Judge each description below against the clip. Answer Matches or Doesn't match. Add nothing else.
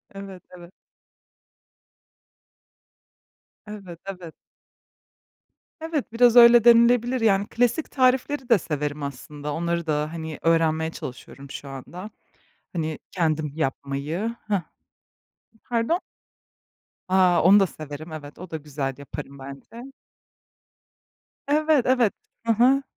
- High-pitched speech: Doesn't match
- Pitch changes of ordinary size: Doesn't match